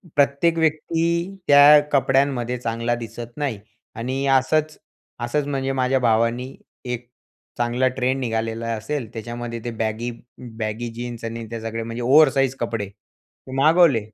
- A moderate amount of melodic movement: Yes, average, 3.2 semitones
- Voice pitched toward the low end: Yes, low, 125 Hz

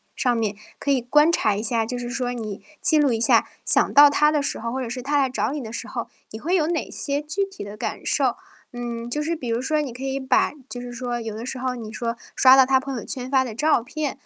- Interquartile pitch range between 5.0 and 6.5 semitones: No, average, 3.6 semitones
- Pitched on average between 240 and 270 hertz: Yes, very high, 255 Hz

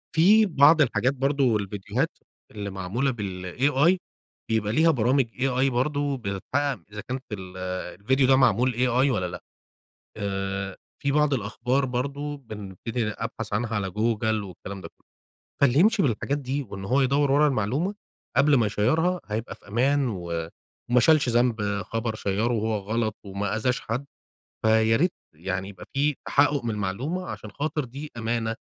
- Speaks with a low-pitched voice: Yes, low, 120 Hz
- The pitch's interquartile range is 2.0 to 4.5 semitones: No, average, 5.2 semitones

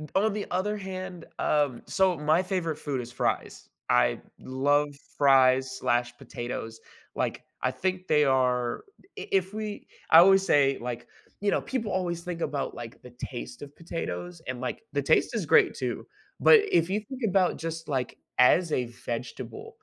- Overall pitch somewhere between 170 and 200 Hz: No, medium, 150 Hz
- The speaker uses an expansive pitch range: Yes, wide, 6.9 semitones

